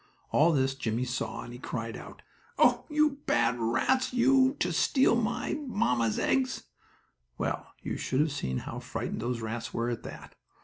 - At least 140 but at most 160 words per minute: No, average, 170 wpm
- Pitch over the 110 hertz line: Yes, low, 135 Hz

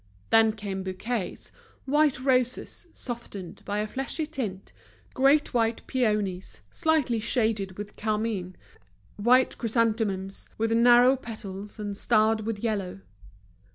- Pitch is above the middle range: Yes, high, 225 Hz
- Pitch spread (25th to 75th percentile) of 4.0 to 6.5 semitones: No, average, 3.4 semitones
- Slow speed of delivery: Yes, slow, 115 wpm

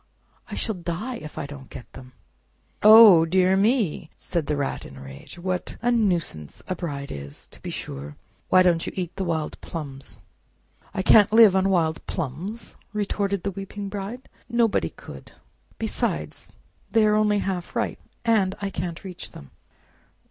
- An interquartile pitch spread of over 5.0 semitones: No, average, 4.7 semitones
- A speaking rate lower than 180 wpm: Yes, average, 165 wpm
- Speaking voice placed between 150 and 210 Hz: Yes, medium, 185 Hz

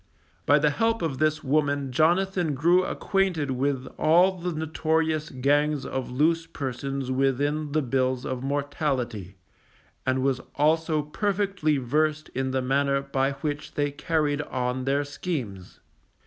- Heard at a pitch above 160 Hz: No, medium, 145 Hz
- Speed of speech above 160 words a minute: No, slow, 135 wpm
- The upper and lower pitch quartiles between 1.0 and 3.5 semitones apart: Yes, average, 3.0 semitones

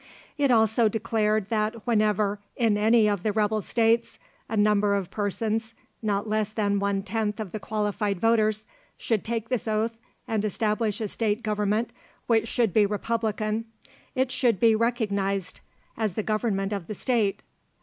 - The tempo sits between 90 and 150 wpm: No, average, 160 wpm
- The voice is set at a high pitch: Yes, high, 215 Hz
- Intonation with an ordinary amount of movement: No, narrow, 1.6 semitones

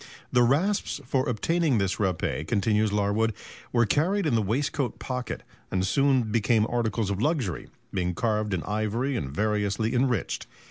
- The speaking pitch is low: Yes, low, 110 Hz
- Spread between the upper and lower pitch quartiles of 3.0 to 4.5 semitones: Yes, average, 4.1 semitones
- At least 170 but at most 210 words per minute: No, average, 150 wpm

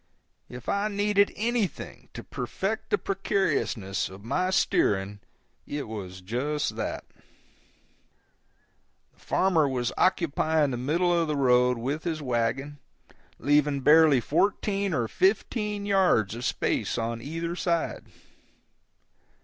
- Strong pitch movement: Yes, wide, 7.4 semitones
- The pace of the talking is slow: Yes, slow, 115 wpm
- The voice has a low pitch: No, medium, 150 Hz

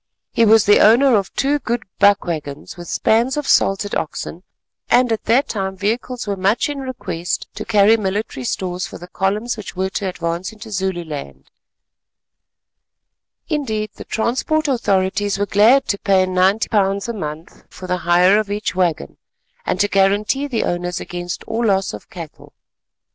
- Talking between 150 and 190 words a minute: Yes, average, 165 wpm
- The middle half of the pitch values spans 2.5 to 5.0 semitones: Yes, average, 3.6 semitones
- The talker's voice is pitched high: Yes, high, 200 Hz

